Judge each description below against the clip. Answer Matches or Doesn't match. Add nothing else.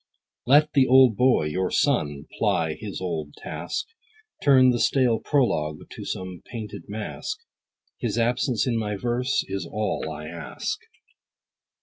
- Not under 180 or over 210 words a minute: Doesn't match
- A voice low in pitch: Matches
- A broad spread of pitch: Matches